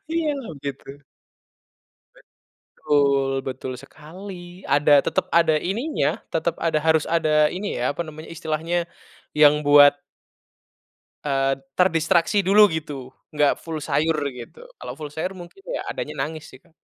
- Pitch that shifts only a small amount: No, average, 3.3 semitones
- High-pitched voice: No, medium, 155 Hz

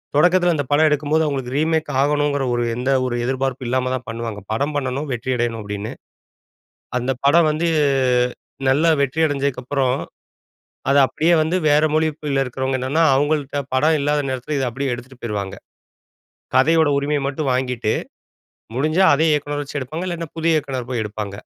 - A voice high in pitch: No, medium, 140 Hz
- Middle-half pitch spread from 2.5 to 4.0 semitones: Yes, average, 3.3 semitones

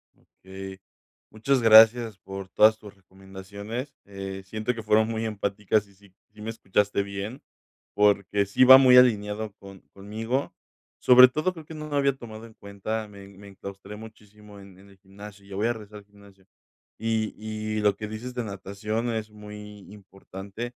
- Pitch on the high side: No, low, 105 Hz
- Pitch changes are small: Yes, narrow, 2.2 semitones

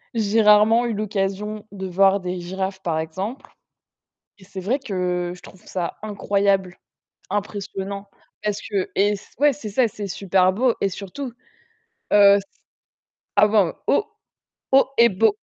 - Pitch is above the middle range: Yes, high, 200 Hz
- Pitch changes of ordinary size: No, narrow, 2.2 semitones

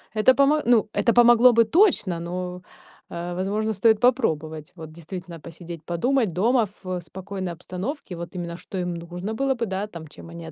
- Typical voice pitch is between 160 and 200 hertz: Yes, medium, 185 Hz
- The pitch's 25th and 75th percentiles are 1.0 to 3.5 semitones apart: No, average, 5.2 semitones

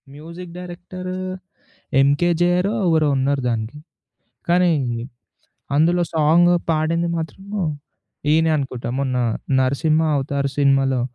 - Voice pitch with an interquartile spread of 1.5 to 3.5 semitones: No, average, 4.0 semitones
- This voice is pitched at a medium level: Yes, medium, 155 Hz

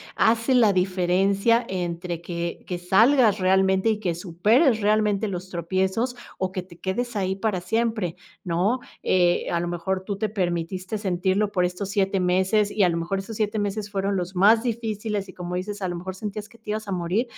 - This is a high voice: Yes, high, 195 Hz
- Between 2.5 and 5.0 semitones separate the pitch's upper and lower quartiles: Yes, average, 3.0 semitones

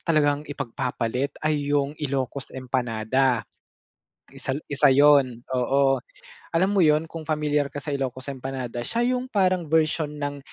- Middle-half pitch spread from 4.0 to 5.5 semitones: No, average, 2.9 semitones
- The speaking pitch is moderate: Yes, medium, 145 Hz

